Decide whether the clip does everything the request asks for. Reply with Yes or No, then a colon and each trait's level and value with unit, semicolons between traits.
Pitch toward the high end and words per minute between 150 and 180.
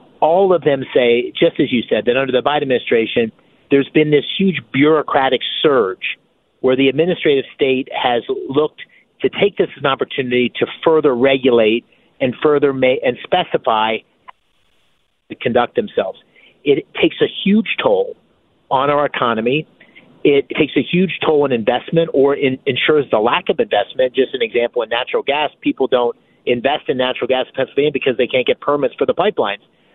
No: medium, 155 Hz; average, 170 wpm